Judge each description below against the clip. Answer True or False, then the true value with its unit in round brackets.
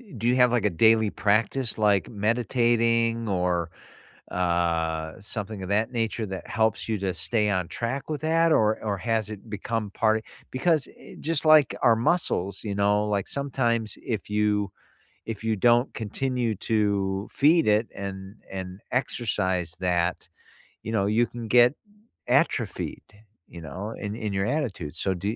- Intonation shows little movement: False (3.3 semitones)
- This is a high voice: False (105 Hz)